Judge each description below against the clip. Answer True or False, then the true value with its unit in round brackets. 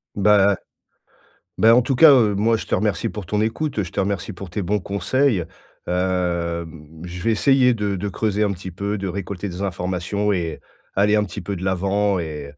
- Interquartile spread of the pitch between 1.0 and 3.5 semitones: True (2.8 semitones)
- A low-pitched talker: True (100 Hz)